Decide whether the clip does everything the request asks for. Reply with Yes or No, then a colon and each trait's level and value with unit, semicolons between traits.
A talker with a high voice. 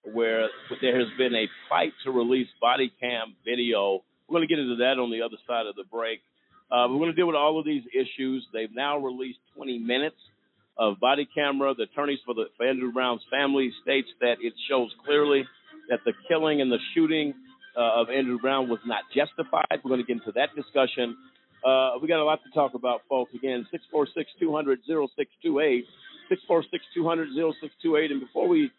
No: low, 135 Hz